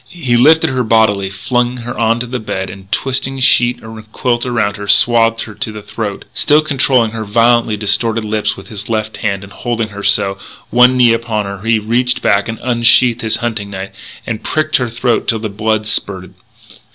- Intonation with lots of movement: No, narrow, 2.6 semitones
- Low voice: Yes, low, 115 Hz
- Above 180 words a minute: Yes, average, 190 wpm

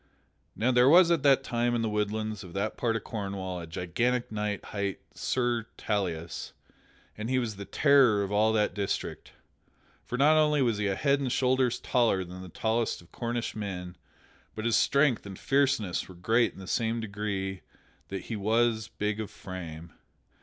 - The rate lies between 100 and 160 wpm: No, average, 180 wpm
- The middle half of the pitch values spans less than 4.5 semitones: Yes, average, 3.8 semitones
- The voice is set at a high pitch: No, low, 110 Hz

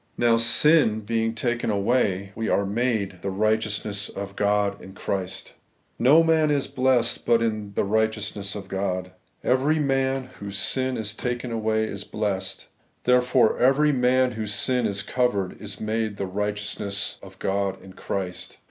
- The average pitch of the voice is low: Yes, low, 110 Hz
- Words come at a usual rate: Yes, average, 155 wpm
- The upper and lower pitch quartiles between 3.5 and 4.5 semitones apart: Yes, average, 3.8 semitones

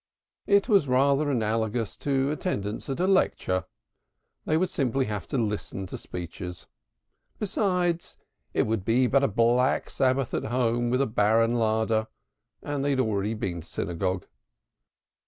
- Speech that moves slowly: No, average, 150 wpm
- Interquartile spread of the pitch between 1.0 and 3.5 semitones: No, average, 4.5 semitones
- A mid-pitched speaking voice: No, low, 120 Hz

